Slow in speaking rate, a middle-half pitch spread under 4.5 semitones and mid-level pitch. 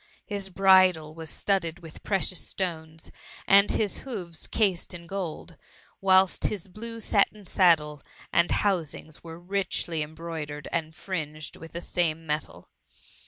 Yes: slow, 130 wpm; average, 3.4 semitones; medium, 170 Hz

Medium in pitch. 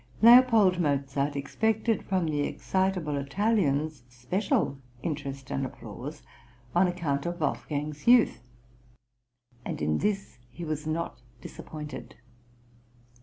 Yes: medium, 155 Hz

